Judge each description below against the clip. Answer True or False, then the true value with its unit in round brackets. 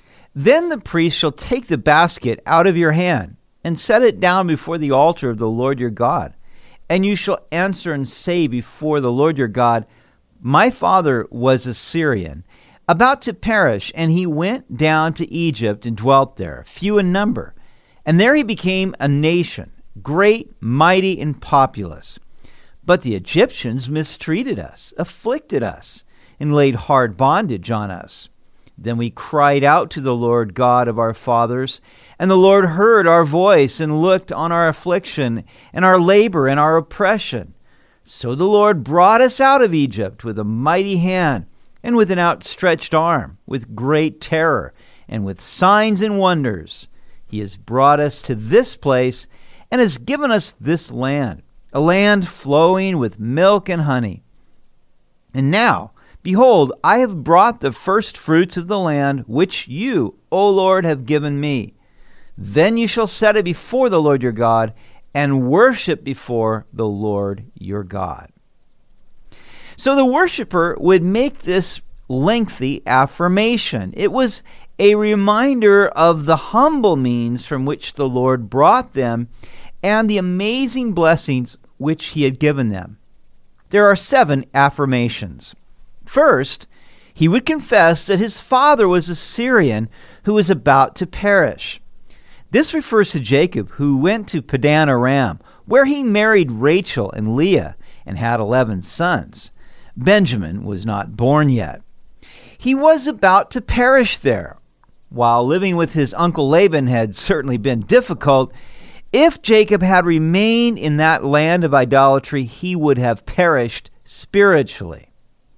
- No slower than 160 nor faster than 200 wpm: False (150 wpm)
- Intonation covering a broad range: True (7.6 semitones)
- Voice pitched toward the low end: False (155 Hz)